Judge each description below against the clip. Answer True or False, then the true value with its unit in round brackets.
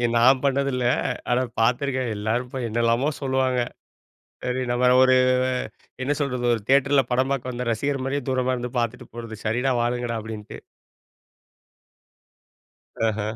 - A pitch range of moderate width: False (2.0 semitones)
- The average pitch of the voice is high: False (125 Hz)